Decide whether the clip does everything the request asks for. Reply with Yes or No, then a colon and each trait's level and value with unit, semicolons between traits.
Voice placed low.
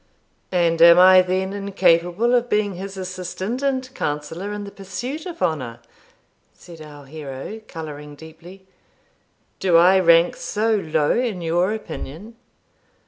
No: medium, 185 Hz